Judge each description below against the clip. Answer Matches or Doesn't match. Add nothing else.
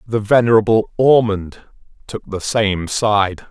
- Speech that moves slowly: Matches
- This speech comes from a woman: Doesn't match